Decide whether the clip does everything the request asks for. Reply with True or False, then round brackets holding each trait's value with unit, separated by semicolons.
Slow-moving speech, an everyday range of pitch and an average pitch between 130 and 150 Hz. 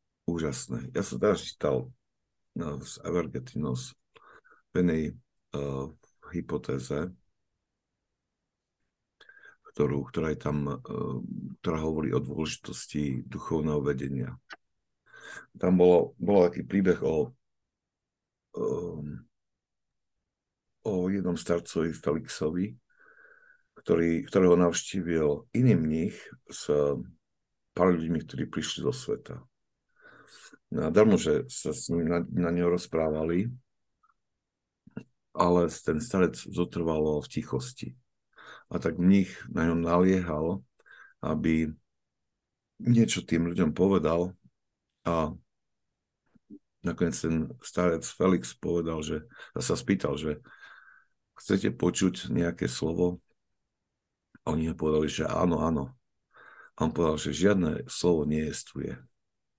False (100 wpm; 3.0 semitones; 80 Hz)